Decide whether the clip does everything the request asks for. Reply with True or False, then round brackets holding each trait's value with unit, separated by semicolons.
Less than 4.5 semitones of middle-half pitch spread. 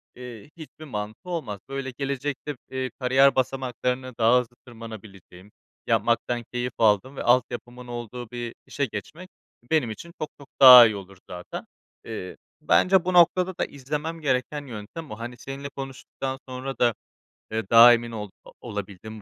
True (3.6 semitones)